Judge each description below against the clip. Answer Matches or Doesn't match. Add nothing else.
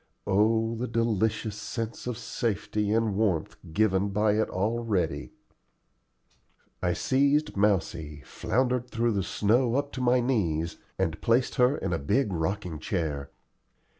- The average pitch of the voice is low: Matches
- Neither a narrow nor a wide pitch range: Matches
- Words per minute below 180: Matches